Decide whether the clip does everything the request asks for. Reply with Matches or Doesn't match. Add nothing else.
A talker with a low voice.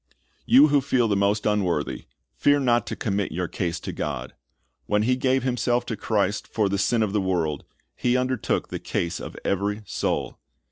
Matches